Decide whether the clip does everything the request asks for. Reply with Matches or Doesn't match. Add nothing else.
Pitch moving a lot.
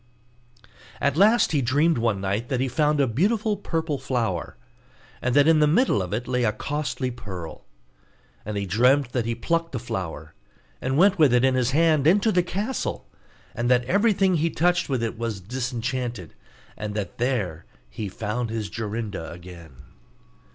Matches